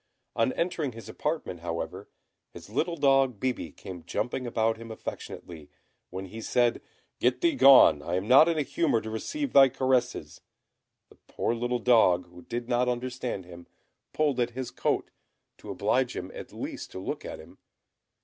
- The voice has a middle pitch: No, low, 120 Hz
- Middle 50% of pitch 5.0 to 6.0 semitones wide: Yes, wide, 5.5 semitones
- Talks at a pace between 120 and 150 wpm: No, average, 170 wpm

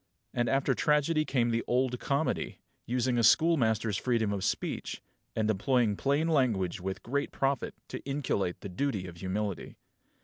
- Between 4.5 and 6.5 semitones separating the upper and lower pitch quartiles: Yes, average, 5.2 semitones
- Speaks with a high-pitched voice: No, low, 120 Hz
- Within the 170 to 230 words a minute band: No, average, 150 wpm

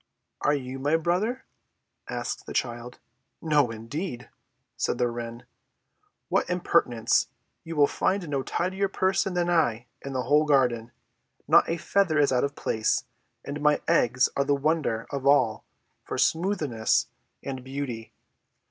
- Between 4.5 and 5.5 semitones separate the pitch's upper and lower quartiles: Yes, average, 5.1 semitones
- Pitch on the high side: No, medium, 140 Hz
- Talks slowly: No, average, 145 wpm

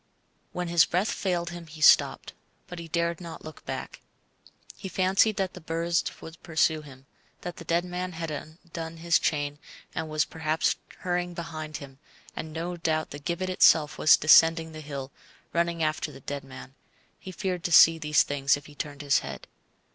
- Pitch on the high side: No, medium, 165 Hz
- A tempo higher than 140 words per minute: Yes, average, 185 wpm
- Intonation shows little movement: Yes, narrow, 2.1 semitones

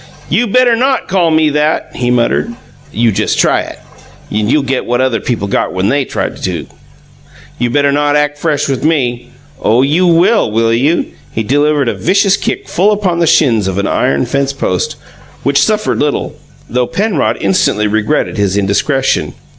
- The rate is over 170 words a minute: Yes, average, 180 wpm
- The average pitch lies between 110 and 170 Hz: Yes, medium, 140 Hz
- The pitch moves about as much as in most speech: No, wide, 6.1 semitones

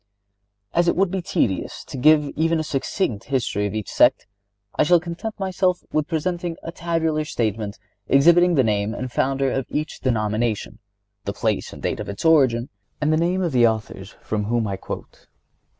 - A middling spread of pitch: No, wide, 7.2 semitones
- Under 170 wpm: No, average, 180 wpm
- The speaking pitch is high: No, medium, 140 Hz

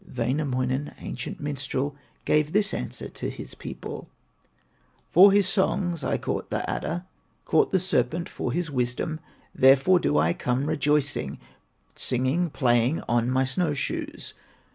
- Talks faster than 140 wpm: No, slow, 135 wpm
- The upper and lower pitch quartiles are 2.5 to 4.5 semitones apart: No, average, 5.3 semitones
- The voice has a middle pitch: Yes, medium, 145 Hz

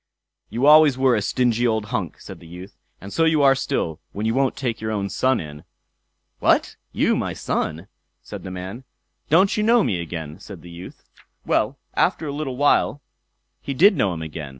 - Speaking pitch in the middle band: No, low, 115 Hz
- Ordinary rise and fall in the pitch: No, wide, 7.6 semitones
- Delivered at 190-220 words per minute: Yes, average, 195 wpm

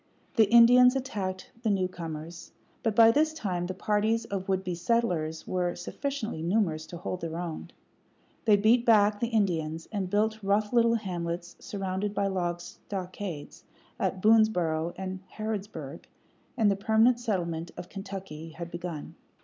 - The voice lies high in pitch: Yes, high, 195 Hz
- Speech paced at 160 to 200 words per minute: No, average, 150 wpm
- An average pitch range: Yes, average, 4.0 semitones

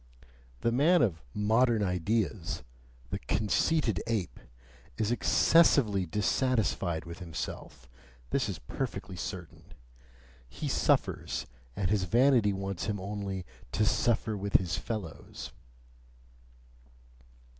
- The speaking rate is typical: No, slow, 100 wpm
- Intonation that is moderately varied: Yes, average, 4.2 semitones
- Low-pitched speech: Yes, low, 105 Hz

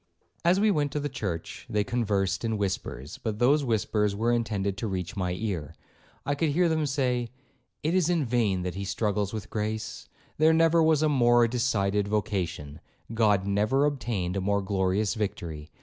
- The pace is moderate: Yes, average, 180 wpm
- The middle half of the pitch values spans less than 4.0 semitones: No, wide, 5.6 semitones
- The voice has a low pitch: Yes, low, 110 Hz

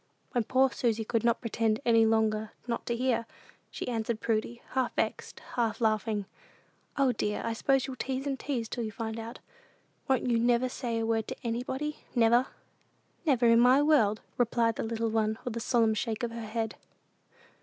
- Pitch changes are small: Yes, narrow, 1.9 semitones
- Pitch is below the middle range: No, high, 230 Hz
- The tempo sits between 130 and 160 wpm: No, average, 185 wpm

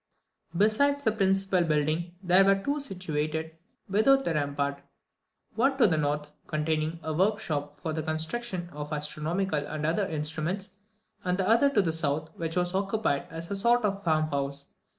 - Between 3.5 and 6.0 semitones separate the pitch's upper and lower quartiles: Yes, average, 4.4 semitones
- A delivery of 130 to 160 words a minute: No, average, 170 wpm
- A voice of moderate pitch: Yes, medium, 170 Hz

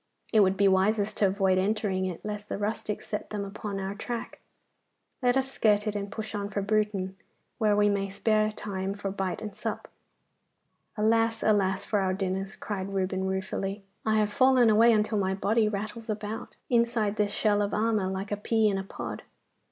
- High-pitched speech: Yes, high, 205 Hz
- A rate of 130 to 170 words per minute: No, average, 190 wpm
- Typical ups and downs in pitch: No, narrow, 1.9 semitones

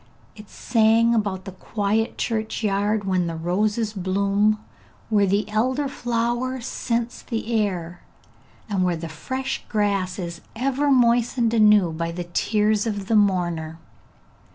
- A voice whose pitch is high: Yes, high, 210 Hz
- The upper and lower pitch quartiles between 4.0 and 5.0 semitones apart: No, average, 3.6 semitones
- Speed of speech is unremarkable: No, slow, 130 wpm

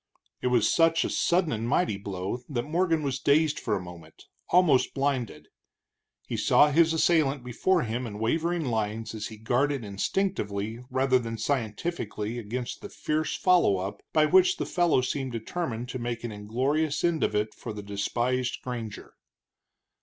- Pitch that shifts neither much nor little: No, wide, 5.9 semitones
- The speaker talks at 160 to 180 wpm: Yes, average, 165 wpm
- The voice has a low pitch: Yes, low, 125 Hz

